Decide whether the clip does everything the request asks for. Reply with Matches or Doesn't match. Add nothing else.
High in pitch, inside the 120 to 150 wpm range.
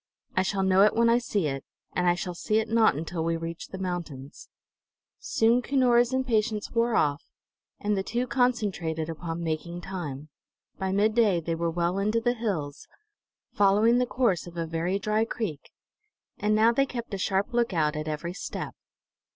Doesn't match